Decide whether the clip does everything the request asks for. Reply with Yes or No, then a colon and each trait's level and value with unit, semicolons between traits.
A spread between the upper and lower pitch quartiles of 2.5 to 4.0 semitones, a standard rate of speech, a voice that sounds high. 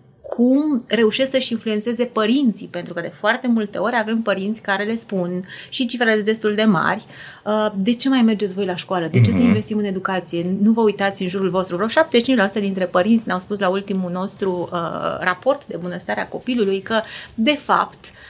No: average, 3.5 semitones; fast, 195 wpm; high, 210 Hz